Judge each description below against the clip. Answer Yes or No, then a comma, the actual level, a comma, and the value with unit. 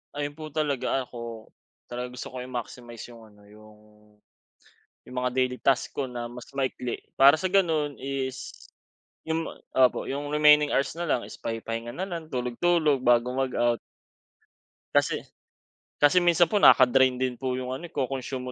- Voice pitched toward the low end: Yes, low, 130 Hz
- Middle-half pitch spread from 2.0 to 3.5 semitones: Yes, average, 3.2 semitones